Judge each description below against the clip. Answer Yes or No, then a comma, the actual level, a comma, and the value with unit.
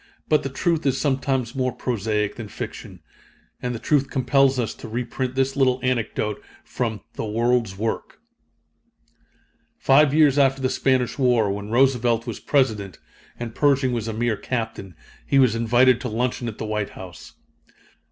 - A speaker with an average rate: Yes, average, 160 wpm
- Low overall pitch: Yes, low, 125 Hz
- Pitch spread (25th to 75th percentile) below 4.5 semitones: Yes, average, 3.1 semitones